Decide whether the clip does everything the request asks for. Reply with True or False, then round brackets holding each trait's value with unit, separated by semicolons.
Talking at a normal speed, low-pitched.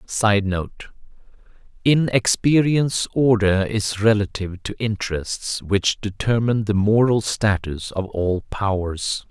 False (105 wpm; 105 Hz)